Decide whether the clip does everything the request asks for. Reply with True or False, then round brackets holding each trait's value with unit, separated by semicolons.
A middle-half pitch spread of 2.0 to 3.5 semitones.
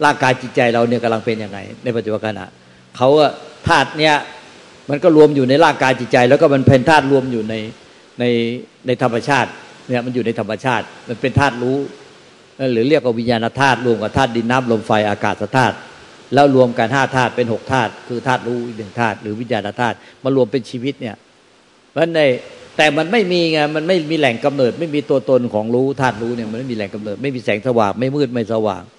True (3.0 semitones)